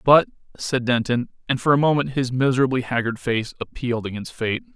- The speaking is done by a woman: No, male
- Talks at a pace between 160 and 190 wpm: Yes, average, 175 wpm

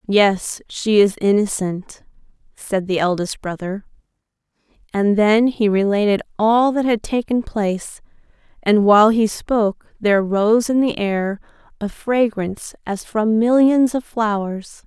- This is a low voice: No, high, 210 Hz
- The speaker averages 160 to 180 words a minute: No, slow, 135 wpm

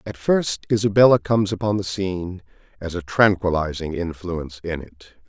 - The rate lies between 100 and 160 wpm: Yes, average, 150 wpm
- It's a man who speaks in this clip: Yes, male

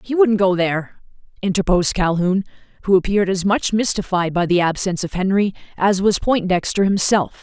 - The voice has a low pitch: No, high, 190 Hz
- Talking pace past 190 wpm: No, average, 160 wpm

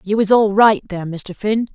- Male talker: No, female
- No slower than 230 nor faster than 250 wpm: Yes, fast, 240 wpm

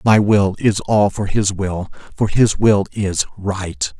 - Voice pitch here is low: Yes, low, 100 Hz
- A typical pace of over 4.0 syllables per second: No, 3.6 syllables/s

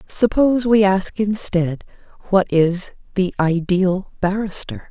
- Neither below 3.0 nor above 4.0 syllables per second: Yes, 3.8 syllables/s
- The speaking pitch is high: Yes, high, 195 Hz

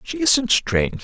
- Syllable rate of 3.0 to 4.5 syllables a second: Yes, 4.1 syllables/s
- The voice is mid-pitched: Yes, medium, 145 Hz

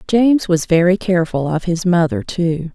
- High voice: No, medium, 180 Hz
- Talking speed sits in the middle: Yes, average, 175 wpm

